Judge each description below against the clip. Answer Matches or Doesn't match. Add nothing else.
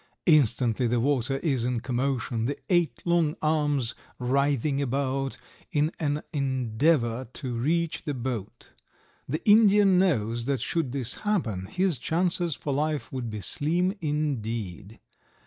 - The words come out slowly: Matches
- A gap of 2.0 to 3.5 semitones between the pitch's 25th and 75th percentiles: Doesn't match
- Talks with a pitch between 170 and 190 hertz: Doesn't match